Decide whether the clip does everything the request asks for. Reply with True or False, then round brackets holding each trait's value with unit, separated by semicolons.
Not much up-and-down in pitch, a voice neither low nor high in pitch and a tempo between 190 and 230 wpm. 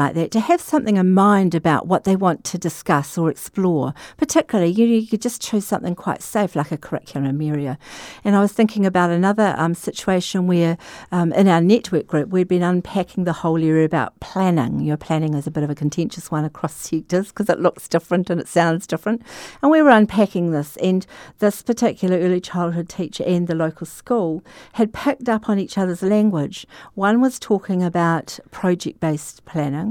False (4.0 semitones; 180 Hz; 195 wpm)